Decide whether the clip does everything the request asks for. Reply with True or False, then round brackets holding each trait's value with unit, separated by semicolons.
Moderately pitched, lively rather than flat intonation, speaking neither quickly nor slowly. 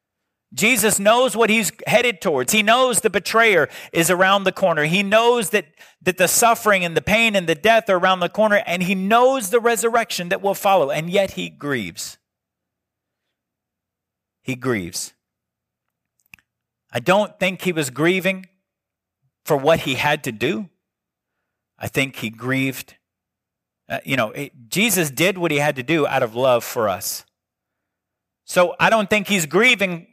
True (180 Hz; 7.4 semitones; 165 wpm)